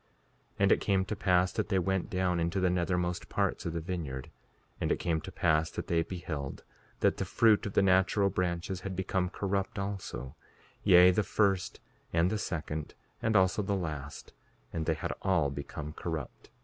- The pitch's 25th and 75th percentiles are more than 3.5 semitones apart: No, average, 2.7 semitones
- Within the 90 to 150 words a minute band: No, average, 190 wpm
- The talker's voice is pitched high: No, very low, 90 Hz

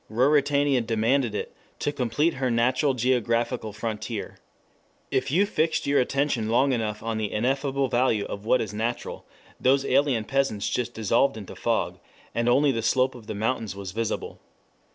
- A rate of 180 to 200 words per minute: No, average, 160 wpm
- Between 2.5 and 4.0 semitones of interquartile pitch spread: Yes, average, 3.6 semitones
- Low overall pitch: Yes, low, 120 Hz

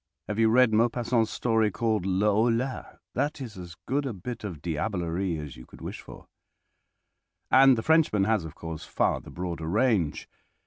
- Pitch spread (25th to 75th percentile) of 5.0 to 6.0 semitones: Yes, wide, 5.4 semitones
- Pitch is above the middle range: No, low, 110 Hz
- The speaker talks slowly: No, average, 175 wpm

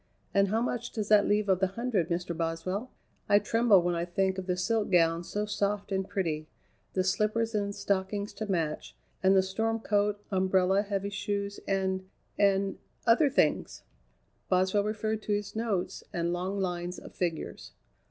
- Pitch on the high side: Yes, high, 195 Hz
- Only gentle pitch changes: Yes, narrow, 2.2 semitones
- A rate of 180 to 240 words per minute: No, average, 170 wpm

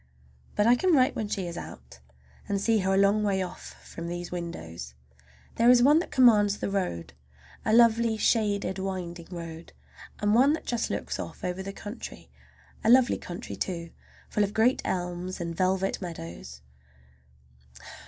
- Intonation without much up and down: No, average, 4.2 semitones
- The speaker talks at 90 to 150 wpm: No, average, 165 wpm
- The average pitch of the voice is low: No, high, 195 Hz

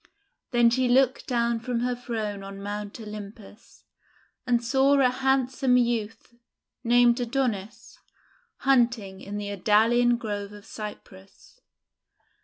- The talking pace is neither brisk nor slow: No, slow, 115 wpm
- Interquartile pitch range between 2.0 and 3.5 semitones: Yes, average, 3.1 semitones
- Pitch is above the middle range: Yes, high, 235 Hz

